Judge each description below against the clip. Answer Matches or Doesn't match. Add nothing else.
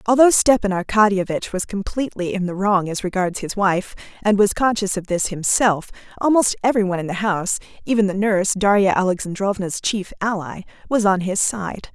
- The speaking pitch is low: Doesn't match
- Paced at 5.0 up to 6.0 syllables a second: Doesn't match